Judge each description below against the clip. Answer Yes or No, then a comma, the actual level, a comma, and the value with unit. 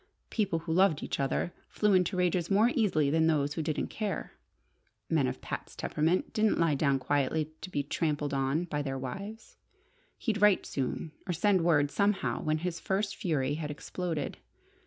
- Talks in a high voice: No, medium, 165 Hz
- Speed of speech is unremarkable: Yes, average, 175 wpm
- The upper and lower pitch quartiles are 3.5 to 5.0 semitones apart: Yes, average, 4.7 semitones